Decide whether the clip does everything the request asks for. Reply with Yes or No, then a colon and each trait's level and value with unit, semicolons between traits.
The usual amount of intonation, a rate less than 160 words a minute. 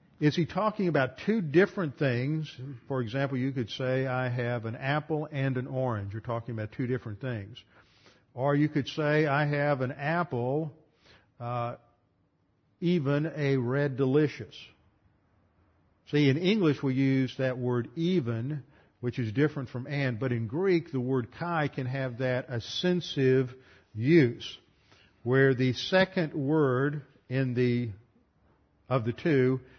Yes: average, 3.7 semitones; average, 145 wpm